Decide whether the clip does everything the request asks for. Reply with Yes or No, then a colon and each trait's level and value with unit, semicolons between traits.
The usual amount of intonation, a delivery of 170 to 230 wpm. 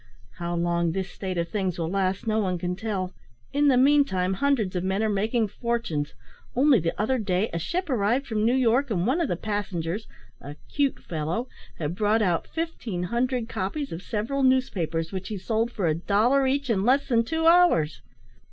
No: wide, 6.0 semitones; average, 195 wpm